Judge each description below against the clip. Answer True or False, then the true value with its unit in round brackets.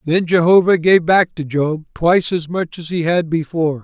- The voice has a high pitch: False (165 Hz)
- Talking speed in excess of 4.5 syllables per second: True (5.0 syllables/s)